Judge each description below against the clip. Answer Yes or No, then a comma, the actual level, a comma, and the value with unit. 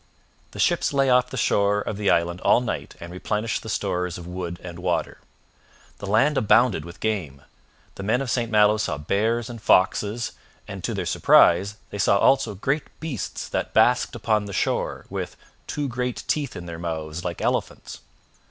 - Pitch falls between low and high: No, low, 105 Hz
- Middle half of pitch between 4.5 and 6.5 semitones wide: Yes, average, 5.1 semitones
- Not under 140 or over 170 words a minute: No, average, 180 wpm